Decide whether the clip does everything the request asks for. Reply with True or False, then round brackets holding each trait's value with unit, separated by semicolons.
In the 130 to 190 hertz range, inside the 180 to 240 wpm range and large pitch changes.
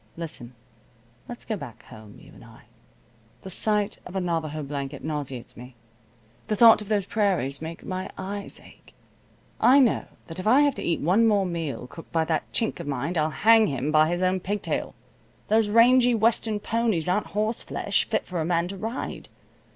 True (185 Hz; 185 wpm; 5.7 semitones)